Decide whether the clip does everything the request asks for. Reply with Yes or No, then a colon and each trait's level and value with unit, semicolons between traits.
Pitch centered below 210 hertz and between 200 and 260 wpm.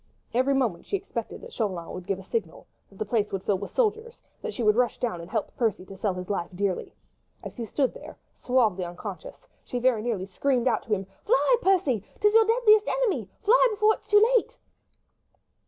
No: high, 240 Hz; fast, 205 wpm